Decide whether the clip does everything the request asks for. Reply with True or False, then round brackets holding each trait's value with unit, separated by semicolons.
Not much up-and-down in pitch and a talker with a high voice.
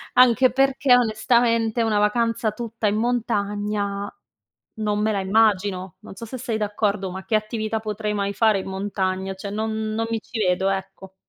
True (2.2 semitones; 215 Hz)